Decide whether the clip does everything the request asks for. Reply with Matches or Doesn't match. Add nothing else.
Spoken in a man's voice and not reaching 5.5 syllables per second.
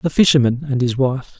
Doesn't match